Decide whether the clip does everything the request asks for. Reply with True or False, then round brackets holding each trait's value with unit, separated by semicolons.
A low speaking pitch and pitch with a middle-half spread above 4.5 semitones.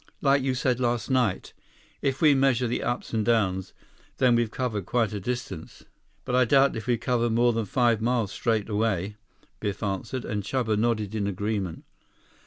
False (115 Hz; 3.2 semitones)